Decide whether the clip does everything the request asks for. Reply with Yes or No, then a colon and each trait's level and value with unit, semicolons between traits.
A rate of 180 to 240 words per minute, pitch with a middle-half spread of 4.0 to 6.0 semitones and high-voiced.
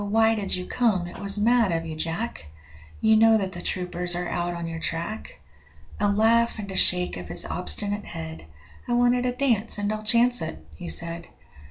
Yes: average, 200 wpm; average, 4.8 semitones; high, 200 Hz